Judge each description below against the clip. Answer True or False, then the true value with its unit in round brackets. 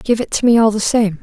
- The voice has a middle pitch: False (220 Hz)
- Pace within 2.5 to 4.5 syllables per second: False (5.9 syllables/s)